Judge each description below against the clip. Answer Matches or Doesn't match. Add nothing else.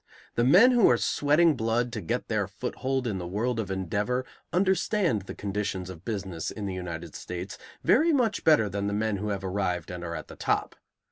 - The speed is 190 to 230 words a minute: Matches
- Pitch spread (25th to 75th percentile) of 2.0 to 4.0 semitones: Doesn't match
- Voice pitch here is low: Matches